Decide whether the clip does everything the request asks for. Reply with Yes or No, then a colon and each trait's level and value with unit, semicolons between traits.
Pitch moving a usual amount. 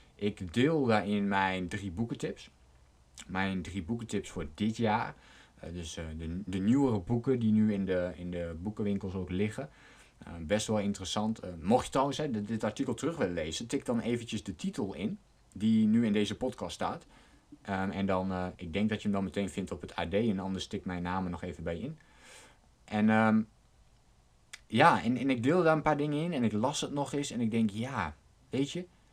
Yes: average, 3.9 semitones